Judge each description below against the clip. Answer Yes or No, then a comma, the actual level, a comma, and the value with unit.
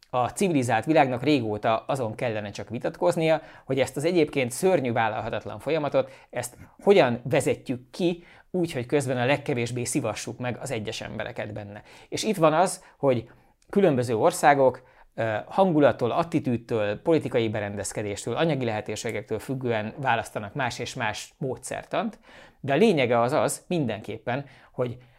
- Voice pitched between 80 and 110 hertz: No, low, 125 Hz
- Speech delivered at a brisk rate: No, average, 135 wpm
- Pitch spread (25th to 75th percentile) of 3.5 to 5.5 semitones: Yes, average, 4.8 semitones